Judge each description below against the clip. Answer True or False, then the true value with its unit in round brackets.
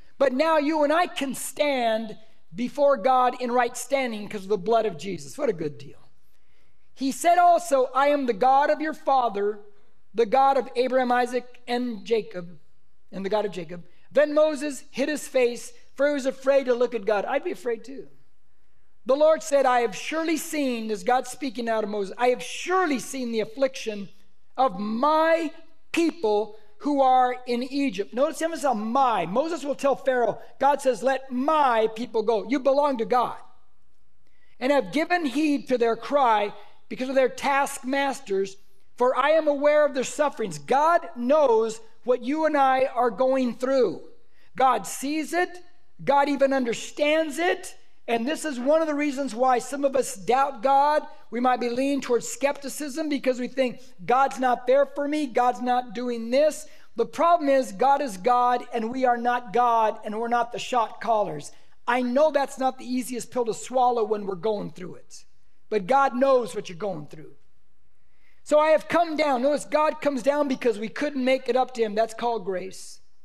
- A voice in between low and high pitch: False (255 Hz)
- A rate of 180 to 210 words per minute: True (190 wpm)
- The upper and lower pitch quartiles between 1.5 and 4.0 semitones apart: True (3.5 semitones)